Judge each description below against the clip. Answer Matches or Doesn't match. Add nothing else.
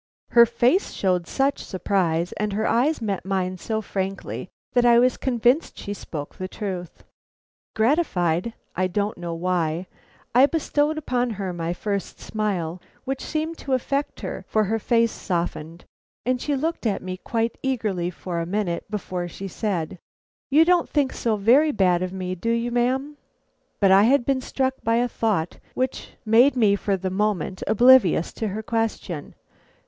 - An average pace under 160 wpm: Doesn't match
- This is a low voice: Doesn't match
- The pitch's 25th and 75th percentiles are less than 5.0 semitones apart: Doesn't match